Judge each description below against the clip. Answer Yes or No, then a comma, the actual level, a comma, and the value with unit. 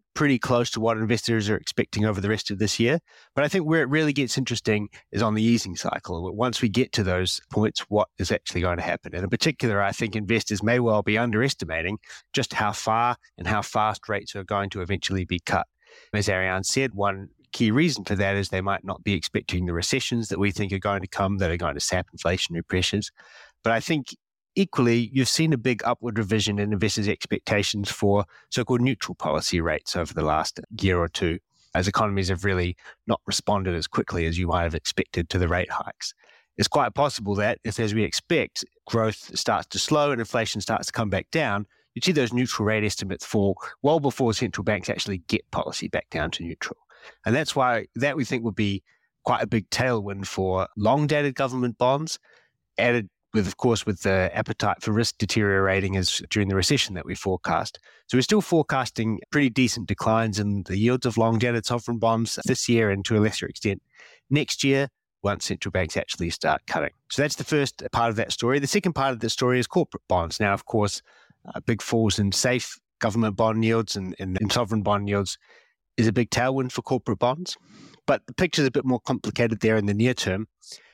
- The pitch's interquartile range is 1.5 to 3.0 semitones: No, average, 3.9 semitones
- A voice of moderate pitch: No, low, 110 Hz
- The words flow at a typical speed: No, fast, 210 wpm